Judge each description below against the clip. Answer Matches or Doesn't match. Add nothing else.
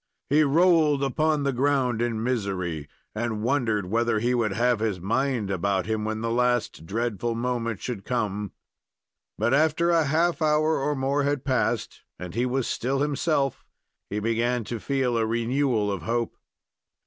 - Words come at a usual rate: Matches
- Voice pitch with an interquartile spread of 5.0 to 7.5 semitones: Doesn't match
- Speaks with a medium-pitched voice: Doesn't match